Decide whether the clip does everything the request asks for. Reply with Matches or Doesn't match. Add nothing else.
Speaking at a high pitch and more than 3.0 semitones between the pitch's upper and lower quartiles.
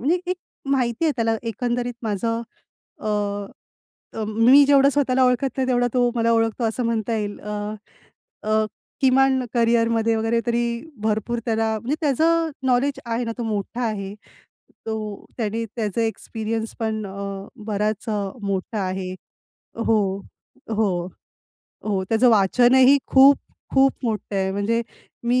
Doesn't match